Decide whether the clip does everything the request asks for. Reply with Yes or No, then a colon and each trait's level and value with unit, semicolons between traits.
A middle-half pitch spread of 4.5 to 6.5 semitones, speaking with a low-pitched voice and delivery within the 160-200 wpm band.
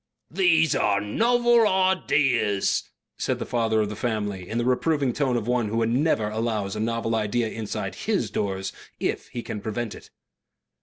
Yes: average, 4.8 semitones; low, 115 Hz; average, 165 wpm